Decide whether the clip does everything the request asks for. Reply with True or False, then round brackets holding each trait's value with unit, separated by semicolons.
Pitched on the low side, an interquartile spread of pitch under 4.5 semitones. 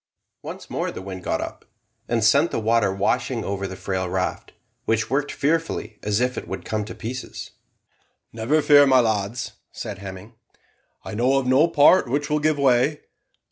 False (120 Hz; 5.5 semitones)